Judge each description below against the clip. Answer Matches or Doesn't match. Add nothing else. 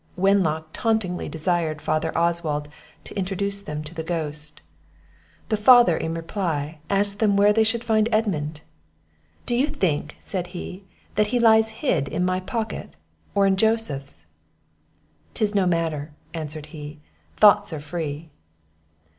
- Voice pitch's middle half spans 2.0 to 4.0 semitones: Doesn't match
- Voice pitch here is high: Doesn't match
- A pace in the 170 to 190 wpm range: Doesn't match